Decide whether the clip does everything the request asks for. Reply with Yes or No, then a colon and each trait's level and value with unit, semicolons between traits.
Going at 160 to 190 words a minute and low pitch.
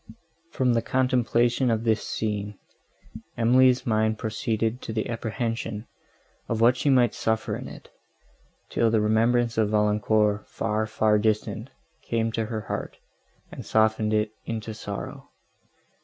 No: slow, 135 wpm; low, 110 Hz